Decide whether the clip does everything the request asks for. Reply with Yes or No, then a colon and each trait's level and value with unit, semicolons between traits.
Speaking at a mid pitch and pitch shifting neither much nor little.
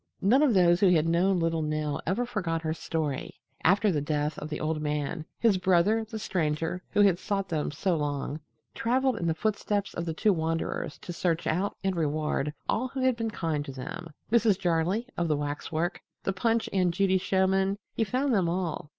Yes: medium, 175 Hz; average, 4.3 semitones